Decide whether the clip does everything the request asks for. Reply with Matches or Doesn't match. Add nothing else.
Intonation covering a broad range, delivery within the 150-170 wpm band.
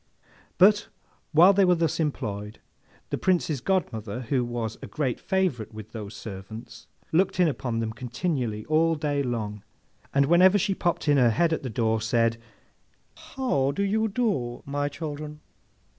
Matches